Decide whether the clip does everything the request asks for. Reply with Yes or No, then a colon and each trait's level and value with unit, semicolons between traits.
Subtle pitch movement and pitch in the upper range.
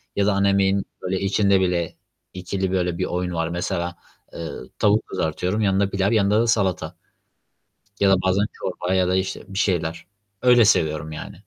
No: narrow, 2.0 semitones; very low, 95 Hz